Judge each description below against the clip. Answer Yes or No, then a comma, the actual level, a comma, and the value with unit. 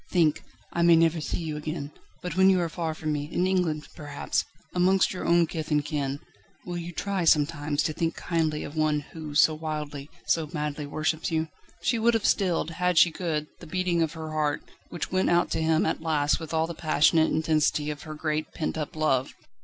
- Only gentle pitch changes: Yes, narrow, 2.1 semitones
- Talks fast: Yes, fast, 210 wpm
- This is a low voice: No, medium, 160 Hz